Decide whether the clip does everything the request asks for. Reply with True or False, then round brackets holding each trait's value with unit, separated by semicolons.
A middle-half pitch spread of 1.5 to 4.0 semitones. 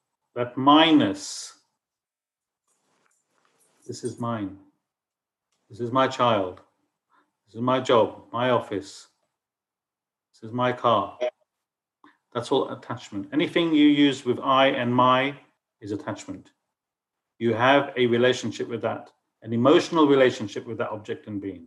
True (3.5 semitones)